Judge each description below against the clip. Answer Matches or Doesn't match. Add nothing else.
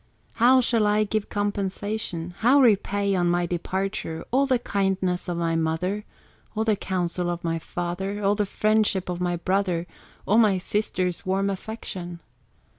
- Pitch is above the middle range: Matches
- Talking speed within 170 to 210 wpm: Doesn't match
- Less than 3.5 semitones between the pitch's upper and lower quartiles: Matches